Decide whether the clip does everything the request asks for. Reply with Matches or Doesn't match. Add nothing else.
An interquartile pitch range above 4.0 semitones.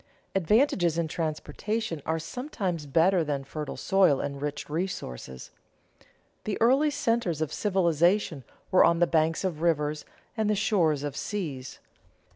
Matches